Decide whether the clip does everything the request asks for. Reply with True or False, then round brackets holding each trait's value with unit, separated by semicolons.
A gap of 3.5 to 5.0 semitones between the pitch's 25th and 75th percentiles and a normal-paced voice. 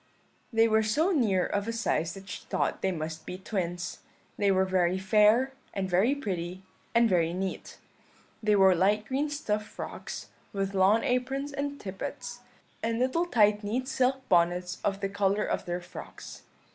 True (4.4 semitones; 170 wpm)